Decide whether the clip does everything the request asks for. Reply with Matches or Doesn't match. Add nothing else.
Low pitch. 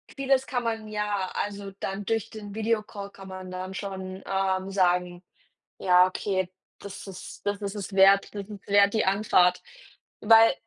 Doesn't match